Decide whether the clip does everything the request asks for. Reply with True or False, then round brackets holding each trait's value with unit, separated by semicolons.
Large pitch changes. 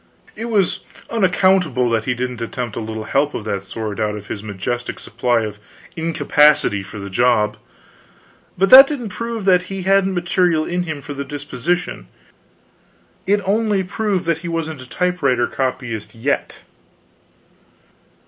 True (8.1 semitones)